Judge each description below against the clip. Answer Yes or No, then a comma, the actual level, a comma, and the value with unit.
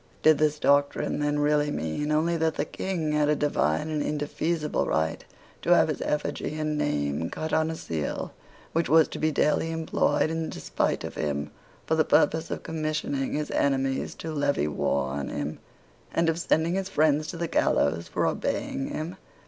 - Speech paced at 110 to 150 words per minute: No, average, 180 wpm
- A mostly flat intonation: Yes, narrow, 2.2 semitones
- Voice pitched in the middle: Yes, medium, 150 Hz